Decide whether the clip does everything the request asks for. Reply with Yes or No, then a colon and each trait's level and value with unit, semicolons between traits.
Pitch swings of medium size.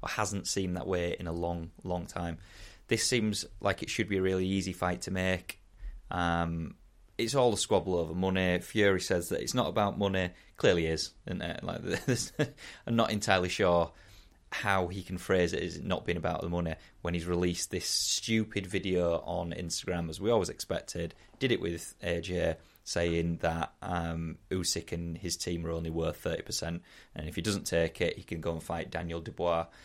No: narrow, 2.3 semitones